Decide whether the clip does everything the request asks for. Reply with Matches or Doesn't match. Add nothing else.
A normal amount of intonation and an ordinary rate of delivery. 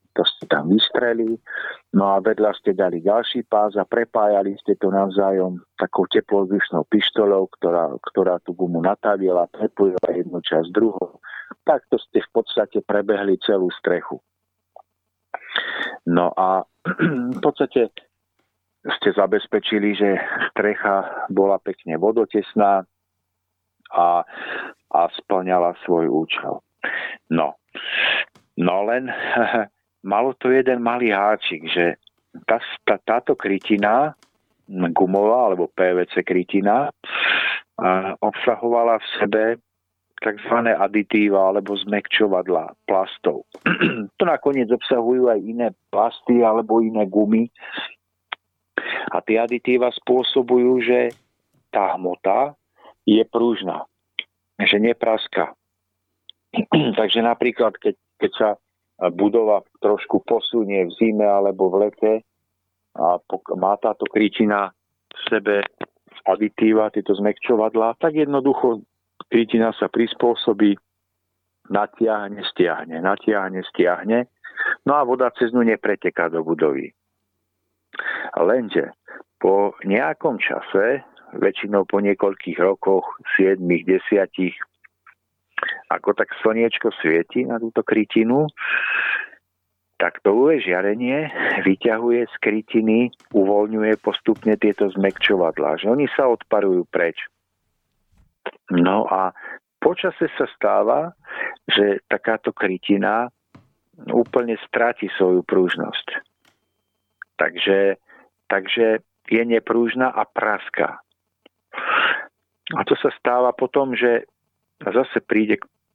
Doesn't match